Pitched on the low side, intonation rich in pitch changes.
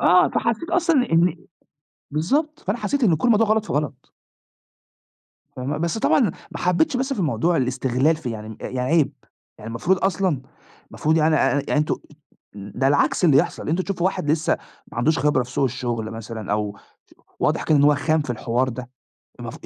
No: medium, 150 Hz; wide, 6.3 semitones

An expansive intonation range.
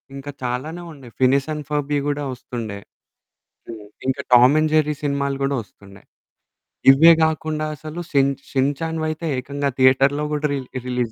No: average, 2.9 semitones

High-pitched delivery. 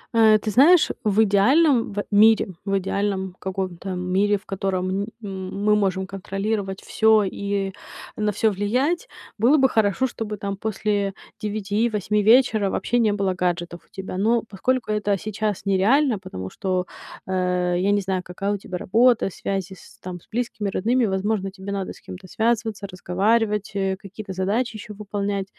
Yes: high, 200 Hz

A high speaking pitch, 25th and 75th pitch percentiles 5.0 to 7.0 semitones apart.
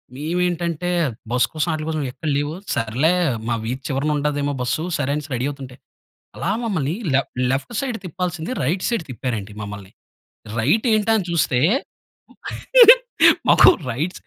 No: medium, 150 Hz; wide, 5.4 semitones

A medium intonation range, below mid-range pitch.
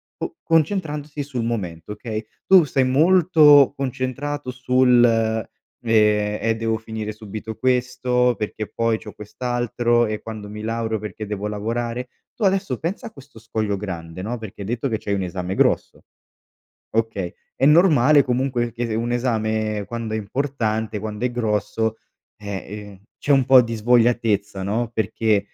Yes: average, 3.1 semitones; low, 115 Hz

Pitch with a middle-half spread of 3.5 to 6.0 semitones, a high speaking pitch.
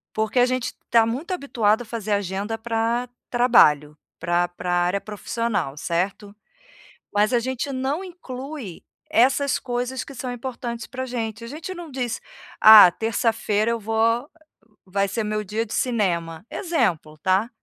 Yes: average, 3.8 semitones; high, 225 Hz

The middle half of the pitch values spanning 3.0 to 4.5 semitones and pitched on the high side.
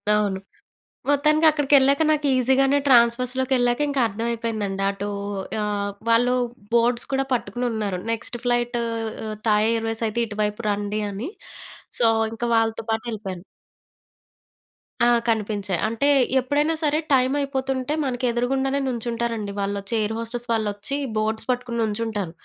Yes: average, 3.6 semitones; high, 235 Hz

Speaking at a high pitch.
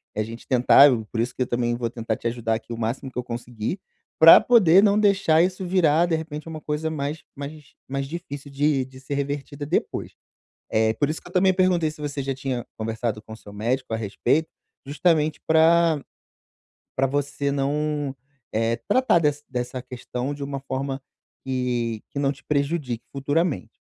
No: medium, 140 Hz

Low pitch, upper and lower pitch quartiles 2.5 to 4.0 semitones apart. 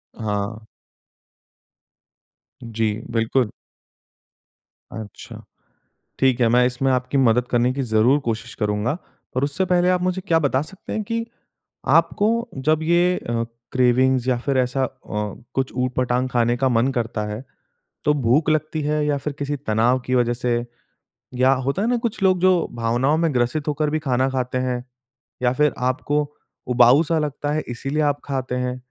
Yes: low, 130 Hz; average, 3.7 semitones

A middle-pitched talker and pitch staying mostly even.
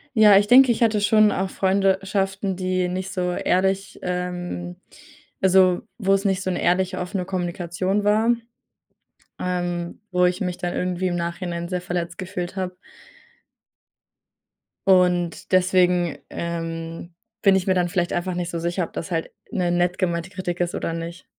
Yes: medium, 180 Hz; narrow, 1.6 semitones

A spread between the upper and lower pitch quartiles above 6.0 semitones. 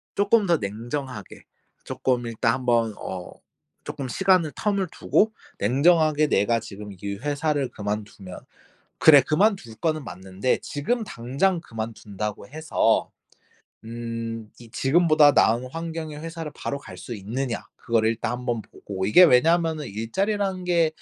Yes: wide, 6.4 semitones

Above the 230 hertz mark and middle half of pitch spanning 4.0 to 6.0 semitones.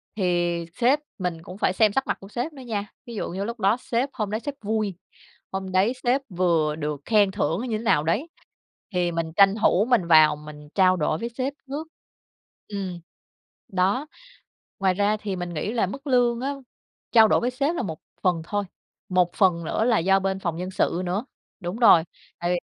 No: high, 195 Hz; average, 4.9 semitones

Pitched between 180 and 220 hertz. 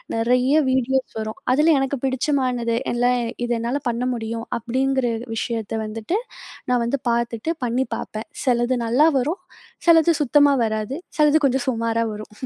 No: high, 245 Hz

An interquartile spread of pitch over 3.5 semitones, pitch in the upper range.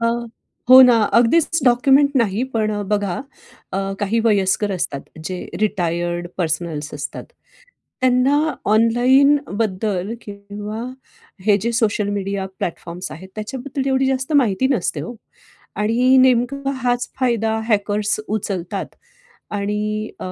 Yes: average, 4.3 semitones; high, 215 Hz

